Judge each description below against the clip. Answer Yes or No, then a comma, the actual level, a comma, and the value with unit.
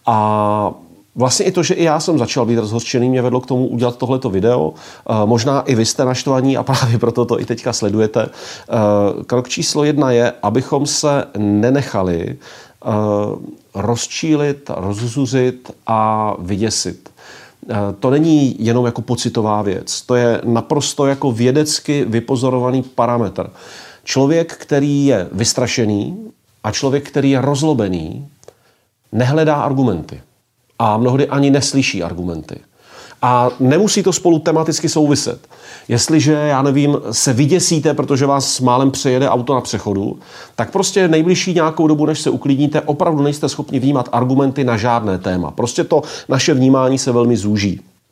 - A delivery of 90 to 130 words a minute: No, average, 140 wpm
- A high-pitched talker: No, low, 130 Hz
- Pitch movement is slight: No, average, 4.0 semitones